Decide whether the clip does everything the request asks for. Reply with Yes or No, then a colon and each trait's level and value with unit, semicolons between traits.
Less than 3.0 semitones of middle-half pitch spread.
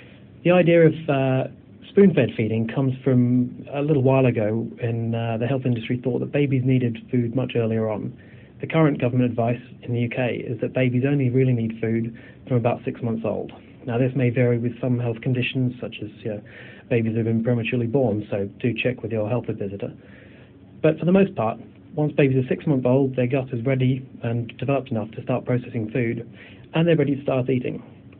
Yes: narrow, 2.5 semitones